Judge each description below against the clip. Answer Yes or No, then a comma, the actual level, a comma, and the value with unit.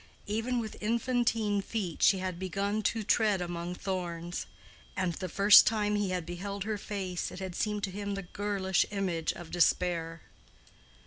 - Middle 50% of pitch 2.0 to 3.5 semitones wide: Yes, average, 2.8 semitones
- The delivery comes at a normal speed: Yes, average, 165 wpm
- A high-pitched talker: Yes, high, 195 Hz